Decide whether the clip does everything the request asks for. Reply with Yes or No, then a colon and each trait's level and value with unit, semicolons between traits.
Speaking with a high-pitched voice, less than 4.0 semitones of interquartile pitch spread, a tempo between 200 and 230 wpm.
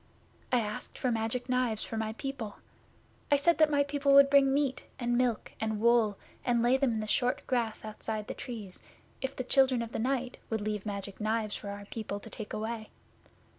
Yes: high, 235 Hz; average, 3.5 semitones; fast, 205 wpm